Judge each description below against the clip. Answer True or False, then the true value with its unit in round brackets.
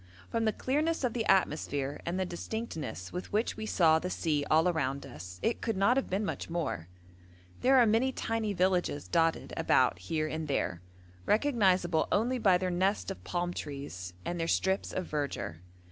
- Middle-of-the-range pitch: True (180 Hz)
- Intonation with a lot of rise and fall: True (6.2 semitones)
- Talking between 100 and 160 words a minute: False (180 wpm)